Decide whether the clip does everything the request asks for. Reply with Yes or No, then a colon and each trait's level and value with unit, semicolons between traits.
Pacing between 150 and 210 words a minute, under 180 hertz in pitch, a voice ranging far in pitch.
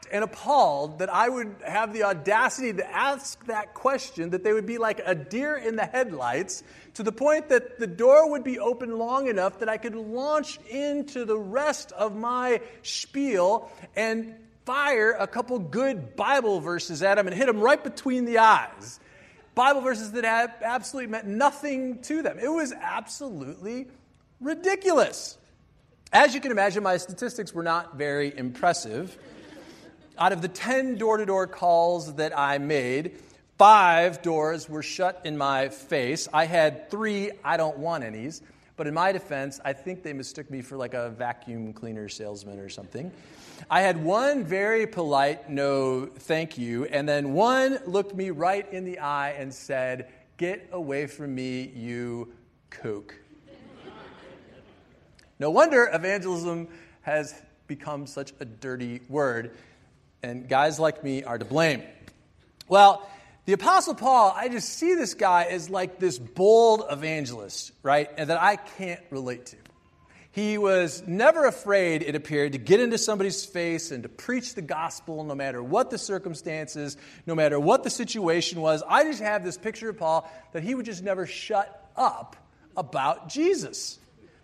No: average, 160 wpm; medium, 185 Hz; wide, 7.9 semitones